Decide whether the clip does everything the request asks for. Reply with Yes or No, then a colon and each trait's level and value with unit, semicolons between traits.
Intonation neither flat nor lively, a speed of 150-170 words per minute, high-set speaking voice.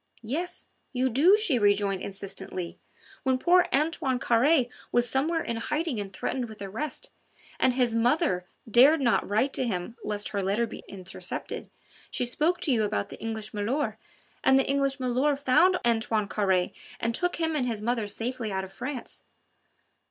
Yes: average, 5.0 semitones; average, 165 wpm; high, 240 Hz